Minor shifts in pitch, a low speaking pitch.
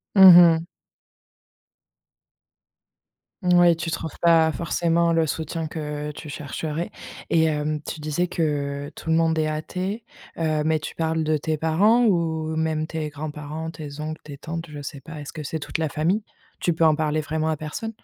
No: narrow, 1.5 semitones; medium, 160 Hz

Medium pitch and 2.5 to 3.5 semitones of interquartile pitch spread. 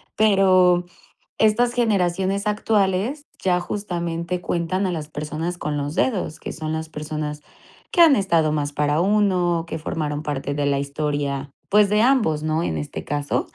No: medium, 170 Hz; average, 4.7 semitones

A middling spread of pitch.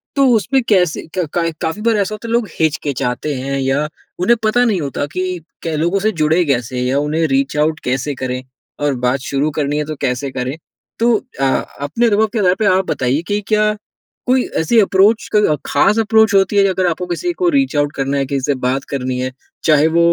No: wide, 7.1 semitones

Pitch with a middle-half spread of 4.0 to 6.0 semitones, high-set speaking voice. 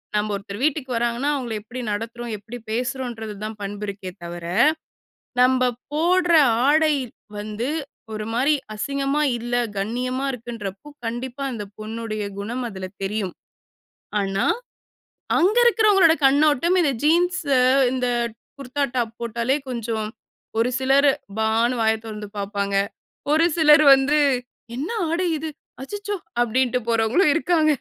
Yes: average, 5.2 semitones; high, 245 Hz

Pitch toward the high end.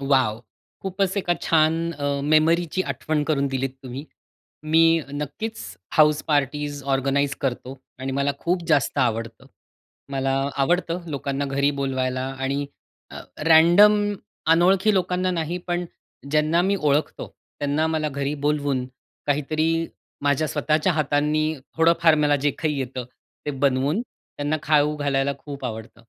No: medium, 150 Hz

